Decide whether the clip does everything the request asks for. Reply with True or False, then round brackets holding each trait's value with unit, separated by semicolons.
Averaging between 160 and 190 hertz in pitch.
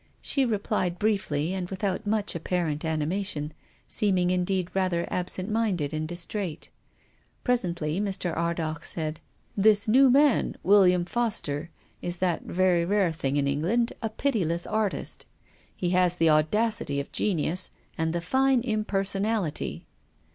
True (185 Hz)